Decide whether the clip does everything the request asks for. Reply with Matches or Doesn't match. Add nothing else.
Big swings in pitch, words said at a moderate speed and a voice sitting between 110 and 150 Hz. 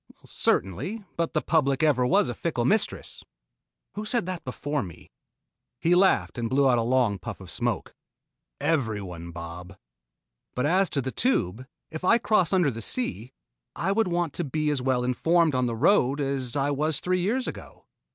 Matches